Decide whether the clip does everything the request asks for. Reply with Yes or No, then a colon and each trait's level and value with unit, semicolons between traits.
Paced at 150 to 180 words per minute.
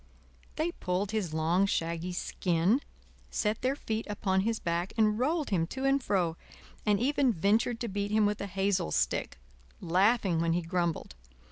Yes: average, 165 wpm